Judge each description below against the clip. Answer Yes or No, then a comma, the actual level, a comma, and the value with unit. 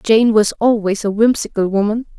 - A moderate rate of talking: Yes, average, 165 wpm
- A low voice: No, high, 215 Hz